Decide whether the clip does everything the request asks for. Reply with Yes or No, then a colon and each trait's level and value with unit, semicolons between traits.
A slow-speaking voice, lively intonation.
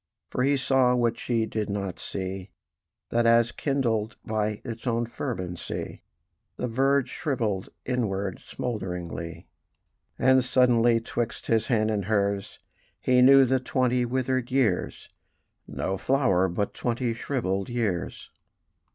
No: slow, 125 wpm; average, 4.0 semitones